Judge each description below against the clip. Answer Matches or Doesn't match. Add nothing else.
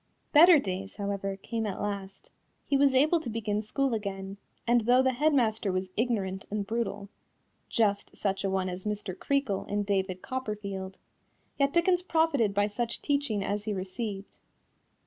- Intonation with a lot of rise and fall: Doesn't match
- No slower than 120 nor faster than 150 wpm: Doesn't match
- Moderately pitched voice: Doesn't match